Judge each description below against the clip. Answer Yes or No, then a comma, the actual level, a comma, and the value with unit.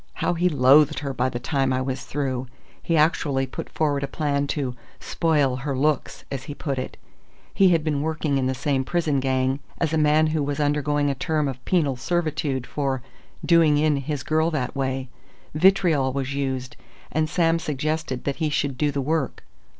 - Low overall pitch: No, medium, 145 Hz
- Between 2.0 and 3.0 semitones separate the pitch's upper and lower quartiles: Yes, average, 2.7 semitones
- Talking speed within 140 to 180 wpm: No, average, 190 wpm